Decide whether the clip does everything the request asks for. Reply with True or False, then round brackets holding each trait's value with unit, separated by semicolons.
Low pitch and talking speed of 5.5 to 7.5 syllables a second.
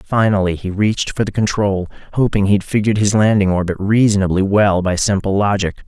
True (100 Hz; 5.8 syllables/s)